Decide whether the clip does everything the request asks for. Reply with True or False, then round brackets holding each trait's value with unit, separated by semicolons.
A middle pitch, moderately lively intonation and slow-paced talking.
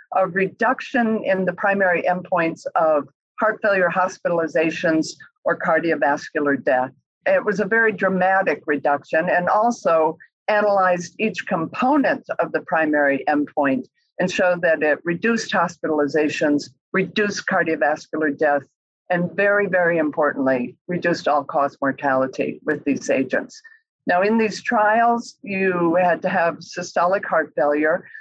True (175 Hz; 4.8 semitones; 125 wpm)